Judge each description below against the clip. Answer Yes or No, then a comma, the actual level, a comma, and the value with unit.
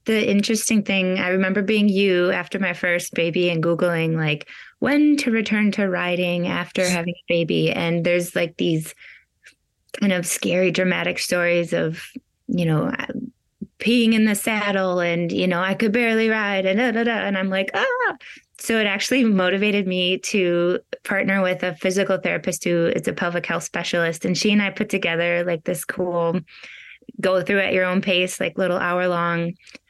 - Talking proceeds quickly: No, average, 180 wpm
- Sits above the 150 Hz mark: Yes, medium, 185 Hz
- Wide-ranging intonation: No, average, 3.0 semitones